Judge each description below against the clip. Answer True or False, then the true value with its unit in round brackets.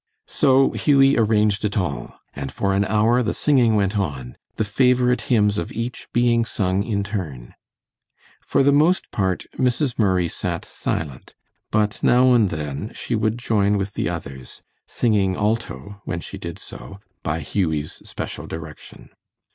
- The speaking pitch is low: True (105 Hz)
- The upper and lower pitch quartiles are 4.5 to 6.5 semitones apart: True (5.1 semitones)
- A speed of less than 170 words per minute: True (155 wpm)